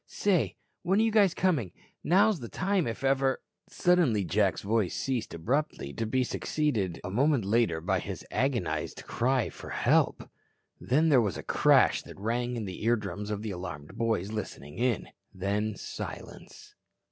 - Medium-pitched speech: No, low, 115 Hz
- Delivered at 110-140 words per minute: No, average, 160 wpm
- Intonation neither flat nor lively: No, wide, 5.7 semitones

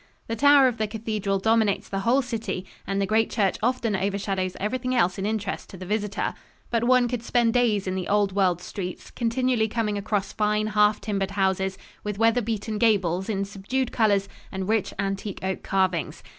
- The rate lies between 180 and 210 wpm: Yes, average, 185 wpm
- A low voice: No, high, 210 Hz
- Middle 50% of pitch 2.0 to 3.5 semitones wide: Yes, average, 2.8 semitones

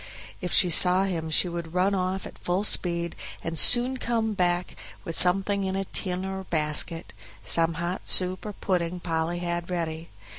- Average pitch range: No, narrow, 2.2 semitones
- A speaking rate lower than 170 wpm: No, average, 175 wpm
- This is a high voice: No, medium, 180 Hz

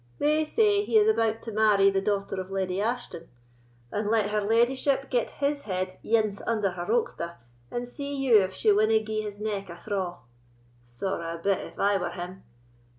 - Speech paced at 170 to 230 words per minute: Yes, average, 190 wpm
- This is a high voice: Yes, high, 210 Hz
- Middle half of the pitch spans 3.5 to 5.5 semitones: Yes, average, 3.8 semitones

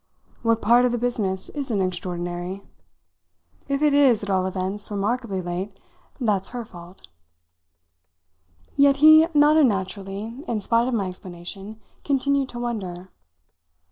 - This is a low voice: No, high, 210 Hz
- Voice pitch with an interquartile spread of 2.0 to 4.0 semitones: No, average, 4.8 semitones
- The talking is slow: Yes, slow, 130 wpm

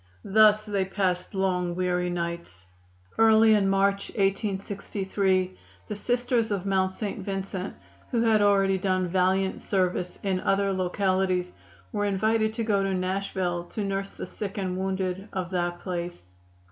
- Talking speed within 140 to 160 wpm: Yes, average, 145 wpm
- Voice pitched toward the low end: No, high, 195 Hz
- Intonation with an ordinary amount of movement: No, narrow, 1.8 semitones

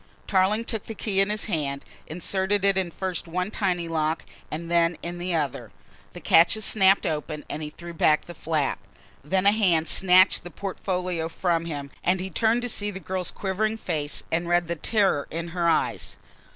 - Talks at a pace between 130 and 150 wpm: No, average, 190 wpm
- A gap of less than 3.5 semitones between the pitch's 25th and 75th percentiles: Yes, average, 3.0 semitones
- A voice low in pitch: No, medium, 175 Hz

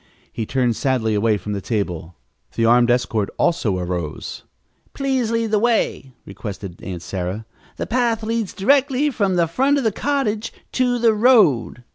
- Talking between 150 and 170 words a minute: Yes, average, 160 wpm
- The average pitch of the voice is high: No, medium, 165 Hz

